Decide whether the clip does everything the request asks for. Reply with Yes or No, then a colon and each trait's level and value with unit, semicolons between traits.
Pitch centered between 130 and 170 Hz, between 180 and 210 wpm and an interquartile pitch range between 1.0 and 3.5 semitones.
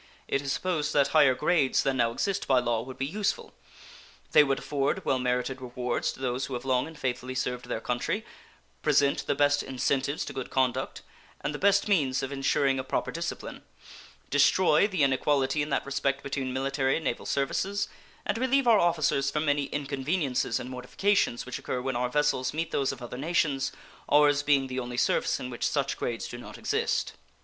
Yes: low, 135 Hz; average, 190 wpm; narrow, 2.6 semitones